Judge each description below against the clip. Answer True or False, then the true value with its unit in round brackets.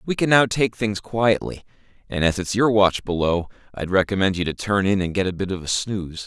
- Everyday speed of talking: False (240 wpm)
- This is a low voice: True (100 Hz)